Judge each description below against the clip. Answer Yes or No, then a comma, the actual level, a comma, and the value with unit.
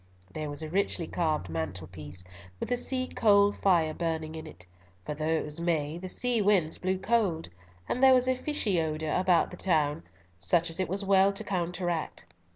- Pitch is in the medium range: Yes, medium, 170 Hz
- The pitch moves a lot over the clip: No, average, 4.3 semitones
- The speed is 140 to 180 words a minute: No, average, 195 wpm